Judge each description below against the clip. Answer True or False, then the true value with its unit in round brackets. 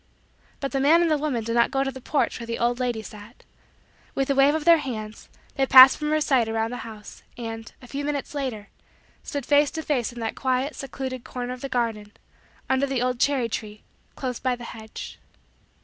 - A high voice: True (255 Hz)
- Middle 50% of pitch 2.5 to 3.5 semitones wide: True (3.2 semitones)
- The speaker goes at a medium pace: False (215 wpm)